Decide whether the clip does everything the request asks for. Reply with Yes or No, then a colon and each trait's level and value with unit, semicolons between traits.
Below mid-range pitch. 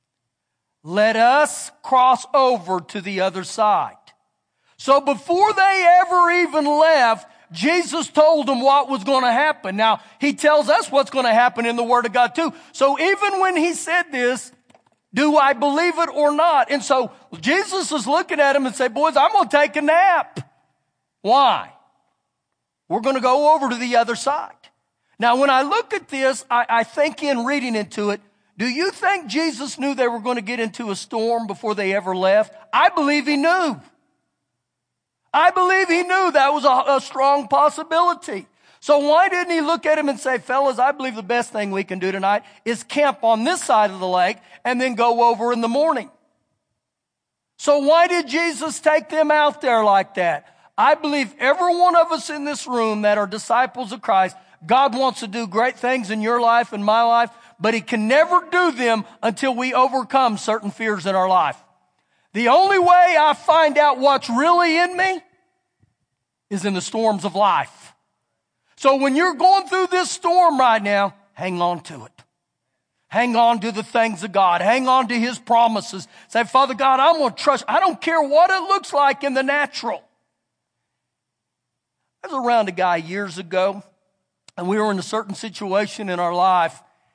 No: very high, 260 Hz